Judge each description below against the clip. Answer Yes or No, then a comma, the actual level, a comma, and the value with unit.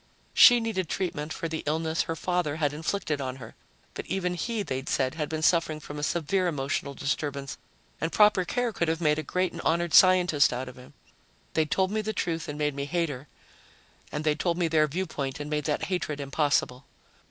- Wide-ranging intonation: No, average, 3.4 semitones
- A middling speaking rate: No, fast, 210 wpm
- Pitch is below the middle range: No, medium, 155 Hz